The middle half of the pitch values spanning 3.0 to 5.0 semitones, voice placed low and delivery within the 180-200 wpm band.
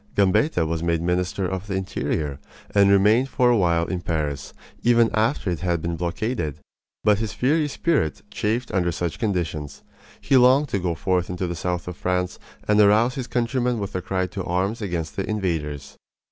Yes: average, 4.5 semitones; very low, 95 Hz; average, 185 wpm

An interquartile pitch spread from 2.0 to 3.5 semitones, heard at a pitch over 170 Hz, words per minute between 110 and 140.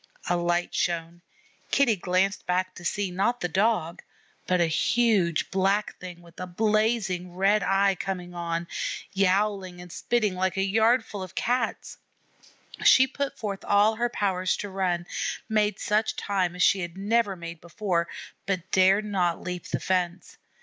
No: average, 2.9 semitones; high, 190 Hz; average, 160 wpm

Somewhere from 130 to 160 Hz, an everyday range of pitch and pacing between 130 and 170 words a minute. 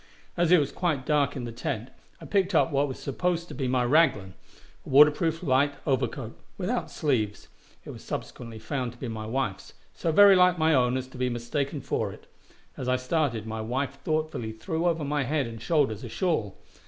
No: low, 135 Hz; average, 4.6 semitones; fast, 205 wpm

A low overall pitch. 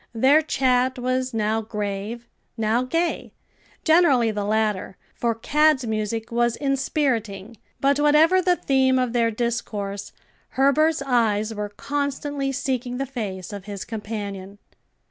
No: high, 240 Hz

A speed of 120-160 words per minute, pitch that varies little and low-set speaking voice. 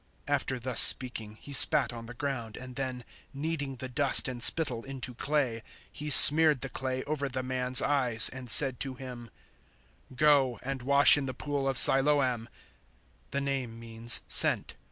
No: average, 175 wpm; narrow, 2.3 semitones; low, 130 Hz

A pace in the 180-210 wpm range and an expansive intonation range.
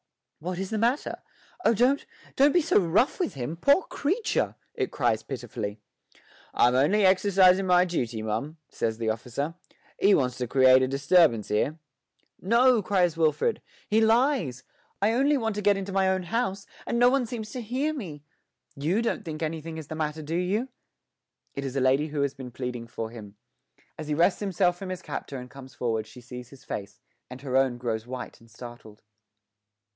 Yes: average, 190 wpm; wide, 8.6 semitones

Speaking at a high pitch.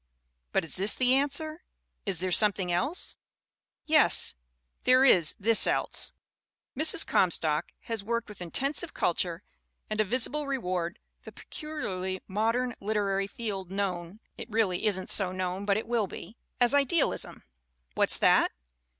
Yes: high, 210 Hz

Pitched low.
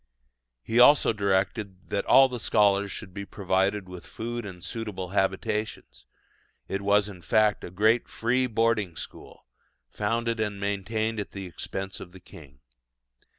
Yes: low, 100 Hz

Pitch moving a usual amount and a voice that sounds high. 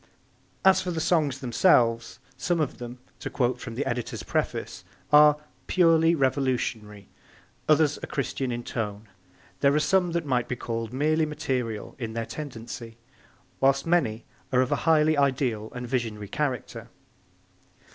No: average, 4.7 semitones; low, 130 Hz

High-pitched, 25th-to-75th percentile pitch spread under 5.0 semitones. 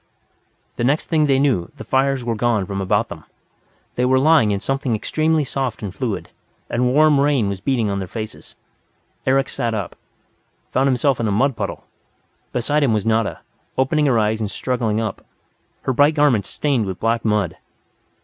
No: low, 120 Hz; average, 4.2 semitones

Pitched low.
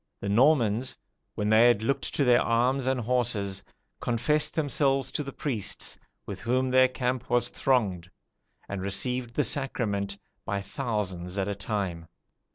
Yes: low, 120 Hz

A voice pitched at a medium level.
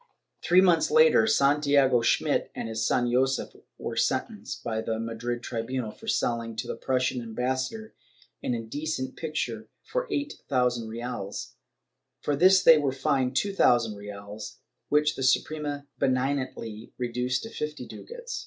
No: low, 130 Hz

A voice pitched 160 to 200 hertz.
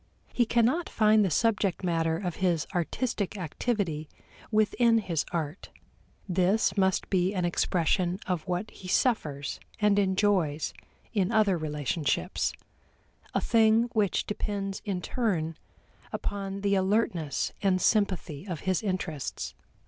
Yes: high, 190 Hz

